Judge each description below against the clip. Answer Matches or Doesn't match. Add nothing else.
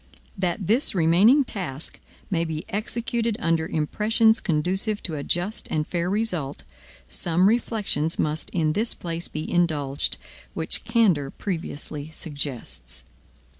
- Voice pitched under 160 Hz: Doesn't match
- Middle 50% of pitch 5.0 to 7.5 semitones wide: Matches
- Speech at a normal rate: Doesn't match